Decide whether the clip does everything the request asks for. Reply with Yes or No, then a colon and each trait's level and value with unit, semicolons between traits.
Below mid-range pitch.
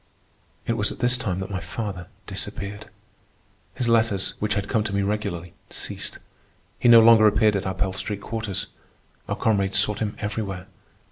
Yes: low, 105 Hz